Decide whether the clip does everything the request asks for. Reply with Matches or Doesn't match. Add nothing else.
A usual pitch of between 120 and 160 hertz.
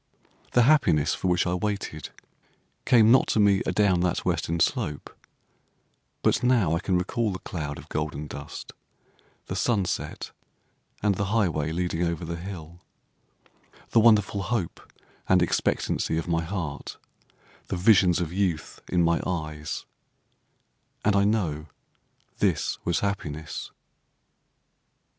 Doesn't match